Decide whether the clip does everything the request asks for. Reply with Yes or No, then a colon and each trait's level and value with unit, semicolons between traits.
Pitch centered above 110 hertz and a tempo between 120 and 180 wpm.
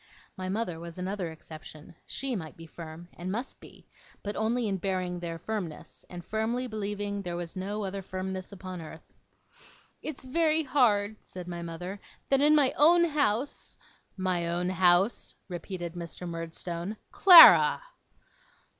Yes: high, 190 Hz; average, 150 wpm